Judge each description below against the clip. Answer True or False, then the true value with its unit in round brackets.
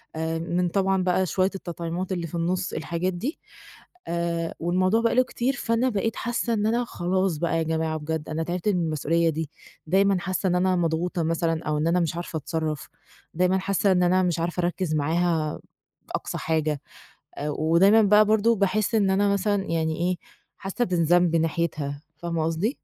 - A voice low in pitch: False (175 Hz)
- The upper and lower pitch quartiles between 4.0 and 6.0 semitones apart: False (2.9 semitones)